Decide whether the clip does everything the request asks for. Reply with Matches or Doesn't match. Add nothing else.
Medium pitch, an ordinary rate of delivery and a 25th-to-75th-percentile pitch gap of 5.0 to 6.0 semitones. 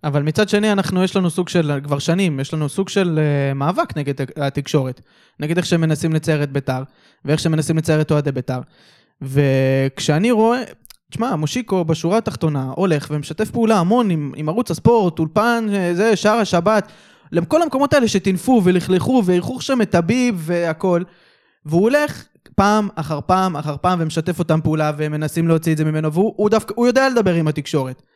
Doesn't match